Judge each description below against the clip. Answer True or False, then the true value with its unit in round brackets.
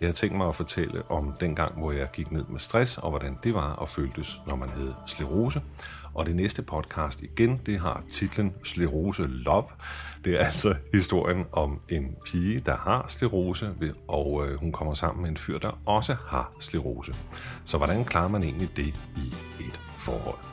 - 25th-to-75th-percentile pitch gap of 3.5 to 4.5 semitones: True (4.0 semitones)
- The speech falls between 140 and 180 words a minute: False (190 wpm)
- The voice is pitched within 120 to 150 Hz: False (80 Hz)